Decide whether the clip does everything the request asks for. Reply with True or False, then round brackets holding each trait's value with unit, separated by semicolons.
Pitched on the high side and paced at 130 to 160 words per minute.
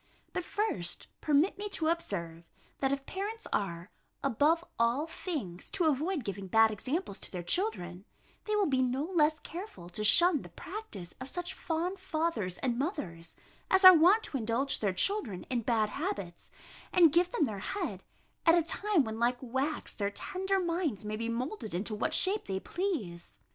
False (275 Hz; 175 wpm)